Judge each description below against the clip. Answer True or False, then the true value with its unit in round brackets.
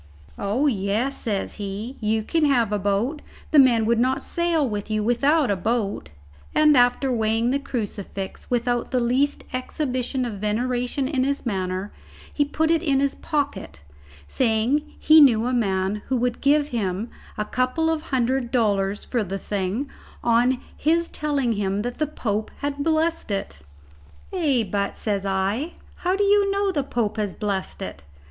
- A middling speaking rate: True (165 wpm)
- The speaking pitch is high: True (245 Hz)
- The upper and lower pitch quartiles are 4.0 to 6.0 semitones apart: True (5.3 semitones)